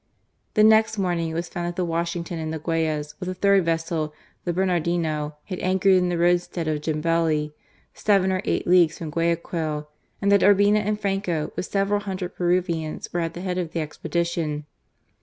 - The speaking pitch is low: No, medium, 170 Hz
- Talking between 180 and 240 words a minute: Yes, average, 185 wpm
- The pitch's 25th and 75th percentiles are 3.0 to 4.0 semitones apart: No, narrow, 2.6 semitones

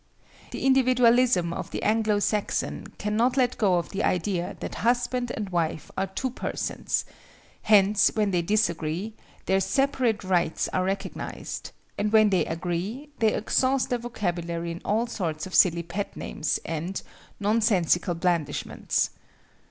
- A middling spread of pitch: Yes, average, 4.7 semitones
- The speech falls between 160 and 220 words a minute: No, slow, 135 wpm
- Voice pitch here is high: Yes, high, 200 Hz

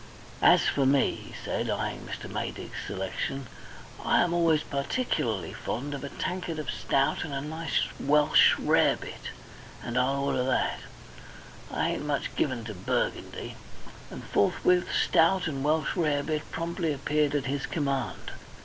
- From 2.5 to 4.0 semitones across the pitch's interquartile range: Yes, average, 2.9 semitones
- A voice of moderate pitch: Yes, medium, 145 Hz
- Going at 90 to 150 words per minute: Yes, average, 145 wpm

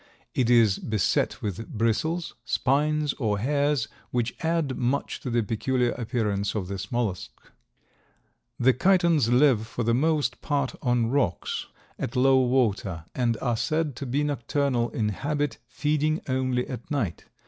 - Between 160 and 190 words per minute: No, average, 145 wpm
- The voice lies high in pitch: No, low, 125 Hz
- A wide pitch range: No, average, 4.1 semitones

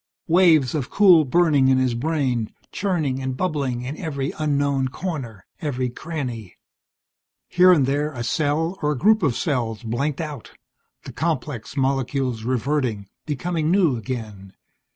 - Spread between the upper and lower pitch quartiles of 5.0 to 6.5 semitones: No, average, 4.1 semitones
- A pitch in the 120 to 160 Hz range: Yes, medium, 140 Hz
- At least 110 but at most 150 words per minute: Yes, average, 140 wpm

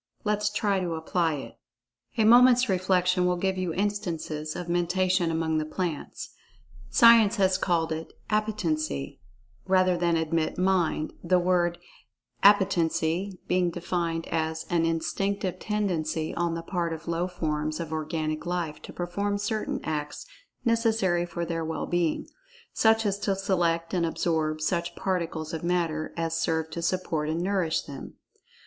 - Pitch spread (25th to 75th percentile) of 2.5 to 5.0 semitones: Yes, average, 2.8 semitones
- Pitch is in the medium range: Yes, medium, 175 Hz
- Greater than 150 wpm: No, average, 145 wpm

